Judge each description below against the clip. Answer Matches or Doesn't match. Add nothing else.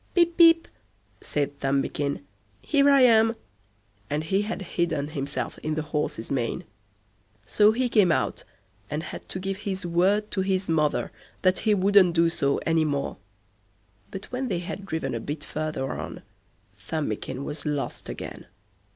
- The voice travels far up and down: Matches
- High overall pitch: Doesn't match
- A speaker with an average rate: Matches